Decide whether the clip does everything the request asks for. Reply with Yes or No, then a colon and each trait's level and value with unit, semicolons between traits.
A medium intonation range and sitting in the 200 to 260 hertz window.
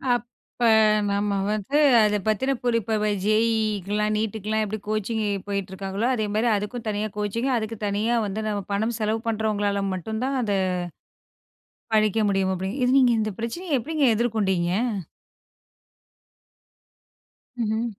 No: narrow, 2.0 semitones; high, 215 Hz